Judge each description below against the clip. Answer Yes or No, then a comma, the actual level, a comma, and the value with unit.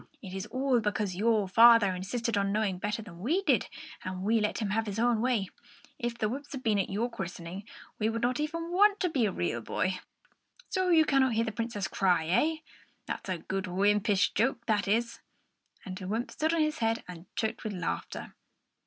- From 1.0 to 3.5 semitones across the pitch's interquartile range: No, average, 4.0 semitones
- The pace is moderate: No, fast, 210 wpm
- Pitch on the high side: Yes, high, 220 Hz